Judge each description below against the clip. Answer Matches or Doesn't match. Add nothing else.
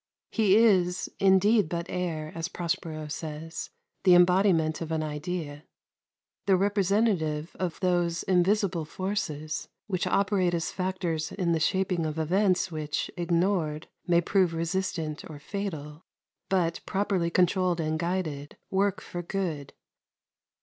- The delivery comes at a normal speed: Doesn't match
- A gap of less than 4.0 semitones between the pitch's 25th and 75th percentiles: Matches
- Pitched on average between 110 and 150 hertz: Doesn't match